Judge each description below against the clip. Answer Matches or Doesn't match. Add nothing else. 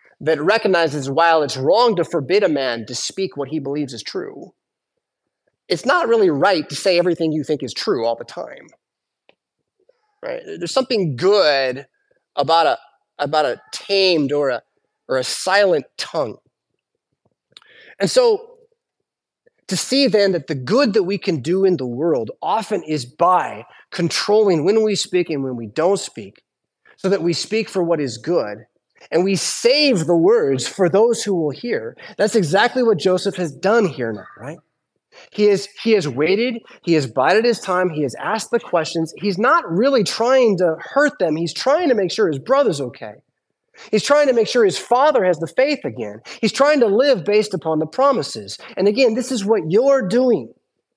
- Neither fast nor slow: Matches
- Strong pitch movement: Matches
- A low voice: Doesn't match